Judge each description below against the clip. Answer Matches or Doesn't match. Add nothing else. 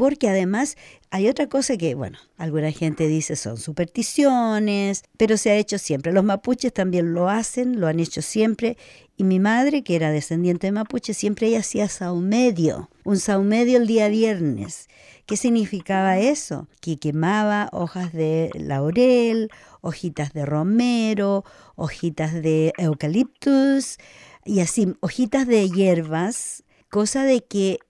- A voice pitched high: Matches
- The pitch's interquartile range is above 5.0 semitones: Matches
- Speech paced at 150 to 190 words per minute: Doesn't match